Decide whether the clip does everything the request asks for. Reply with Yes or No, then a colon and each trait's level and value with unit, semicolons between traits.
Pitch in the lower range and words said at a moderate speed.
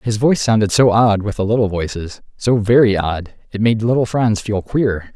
Yes: low, 110 Hz; average, 185 wpm